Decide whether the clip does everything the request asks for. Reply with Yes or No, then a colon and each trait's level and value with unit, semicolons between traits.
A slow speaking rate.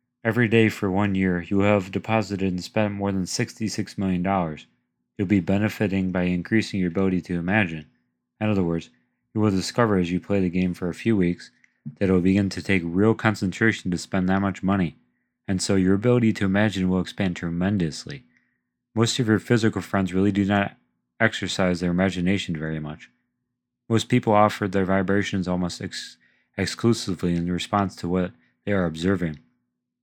No: average, 180 wpm